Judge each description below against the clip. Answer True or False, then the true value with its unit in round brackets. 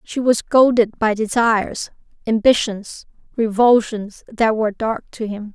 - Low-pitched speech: False (220 Hz)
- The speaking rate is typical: False (130 wpm)